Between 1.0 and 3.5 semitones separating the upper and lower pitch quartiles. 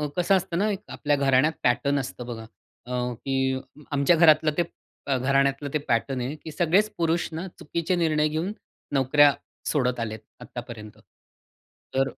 No: average, 4.0 semitones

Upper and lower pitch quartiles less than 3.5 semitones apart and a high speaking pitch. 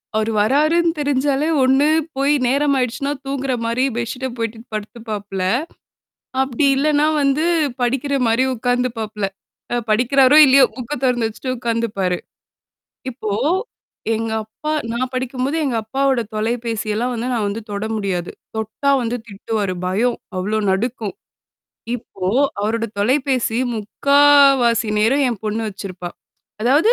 No: average, 3.9 semitones; high, 240 Hz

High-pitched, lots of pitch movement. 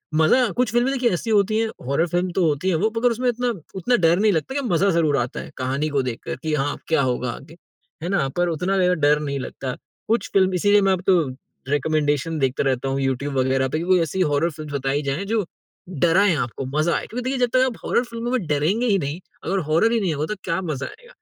No: medium, 170 Hz; wide, 6.3 semitones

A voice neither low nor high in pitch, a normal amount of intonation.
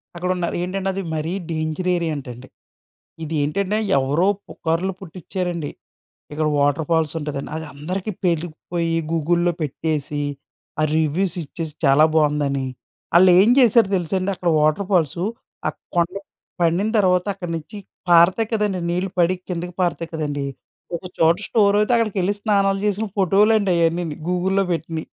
Yes: medium, 175 Hz; average, 3.3 semitones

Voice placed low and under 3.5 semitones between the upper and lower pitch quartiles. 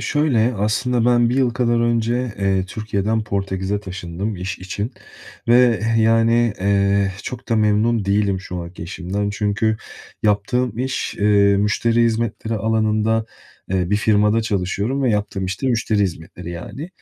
Yes: low, 105 Hz; average, 2.9 semitones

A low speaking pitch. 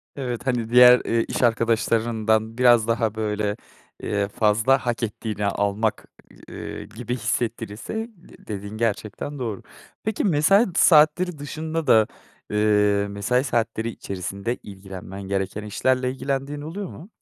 Yes: low, 115 Hz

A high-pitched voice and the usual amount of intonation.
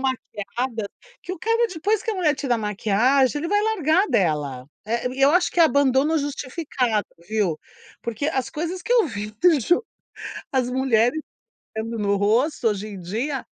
No: very high, 260 Hz; wide, 6.7 semitones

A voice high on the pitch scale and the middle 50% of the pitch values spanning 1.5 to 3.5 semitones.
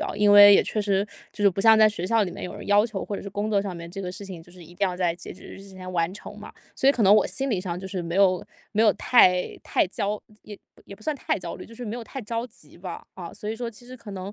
Yes: high, 200 Hz; average, 2.9 semitones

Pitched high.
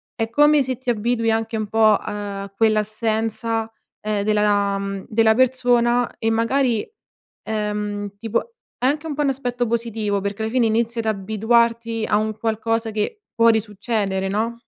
Yes: high, 225 Hz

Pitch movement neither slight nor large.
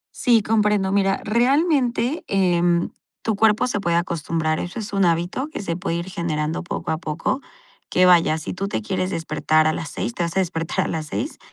Yes: average, 4.2 semitones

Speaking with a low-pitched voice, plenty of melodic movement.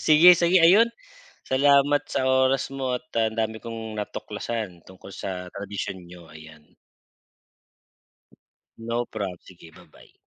Yes: low, 110 Hz; wide, 6.3 semitones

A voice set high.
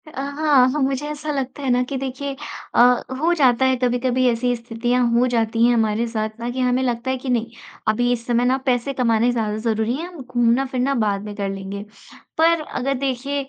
Yes: very high, 250 Hz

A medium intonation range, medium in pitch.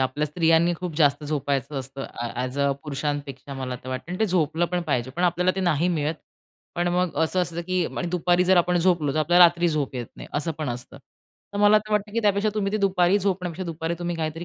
Yes: average, 3.8 semitones; medium, 170 Hz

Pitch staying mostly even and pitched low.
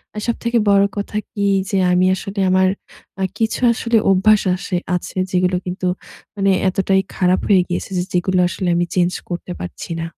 No: narrow, 2.1 semitones; high, 190 Hz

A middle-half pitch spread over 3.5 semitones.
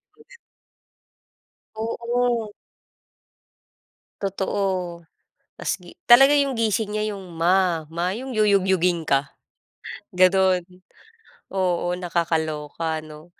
Yes: average, 4.1 semitones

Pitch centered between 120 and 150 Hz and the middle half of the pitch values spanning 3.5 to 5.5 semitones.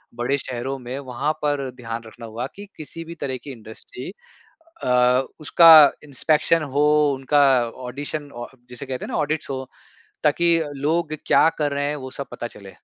No: medium, 140 Hz; average, 3.1 semitones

